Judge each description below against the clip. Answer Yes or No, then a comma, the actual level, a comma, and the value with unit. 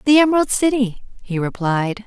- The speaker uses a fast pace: No, average, 145 wpm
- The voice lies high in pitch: Yes, high, 230 Hz